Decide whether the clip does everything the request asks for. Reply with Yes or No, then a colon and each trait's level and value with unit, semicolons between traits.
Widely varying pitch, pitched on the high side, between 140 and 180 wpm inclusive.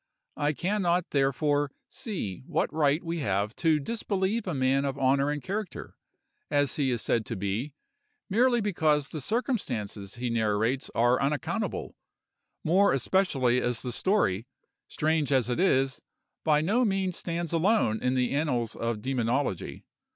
No: wide, 6.3 semitones; medium, 145 Hz; average, 150 wpm